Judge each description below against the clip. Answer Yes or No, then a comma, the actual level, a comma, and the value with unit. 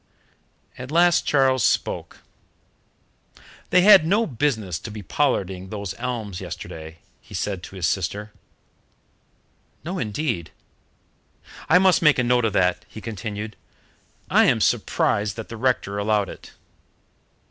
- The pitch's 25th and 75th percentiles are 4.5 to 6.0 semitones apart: Yes, wide, 5.5 semitones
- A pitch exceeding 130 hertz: No, low, 110 Hz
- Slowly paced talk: Yes, slow, 130 wpm